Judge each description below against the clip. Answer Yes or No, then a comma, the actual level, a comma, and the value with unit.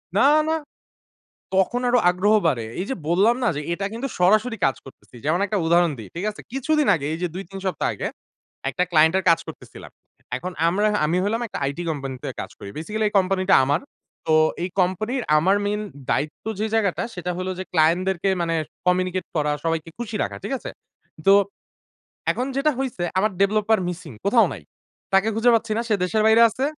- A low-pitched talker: No, high, 190 Hz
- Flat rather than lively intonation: No, average, 4.6 semitones